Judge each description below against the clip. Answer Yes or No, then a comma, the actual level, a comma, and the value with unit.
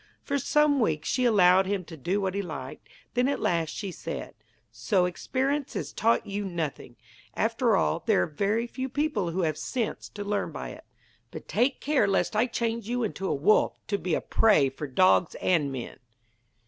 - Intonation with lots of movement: Yes, wide, 6.1 semitones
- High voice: Yes, high, 200 Hz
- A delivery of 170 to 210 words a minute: Yes, average, 195 wpm